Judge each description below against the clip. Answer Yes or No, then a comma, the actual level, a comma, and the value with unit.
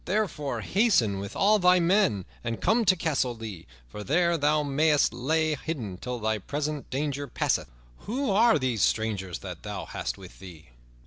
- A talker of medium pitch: Yes, medium, 145 Hz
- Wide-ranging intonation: Yes, wide, 7.9 semitones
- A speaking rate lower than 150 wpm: No, average, 170 wpm